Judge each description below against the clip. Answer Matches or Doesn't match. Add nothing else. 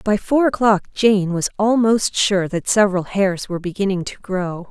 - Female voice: Matches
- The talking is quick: Doesn't match